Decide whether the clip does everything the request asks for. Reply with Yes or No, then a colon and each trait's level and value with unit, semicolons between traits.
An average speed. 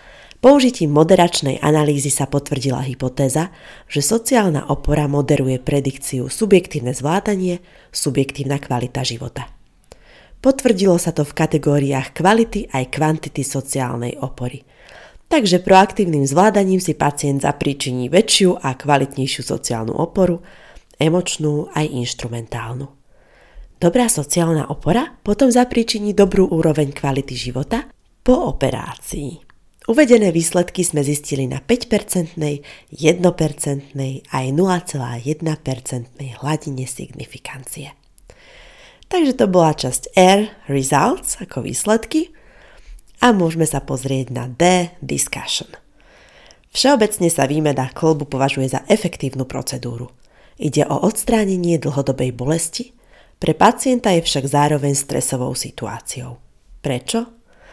No: slow, 105 wpm